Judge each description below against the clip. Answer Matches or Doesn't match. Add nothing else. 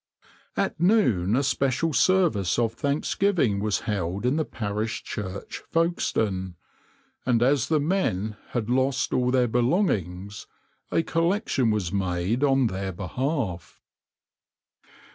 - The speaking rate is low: Matches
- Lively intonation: Matches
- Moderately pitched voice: Doesn't match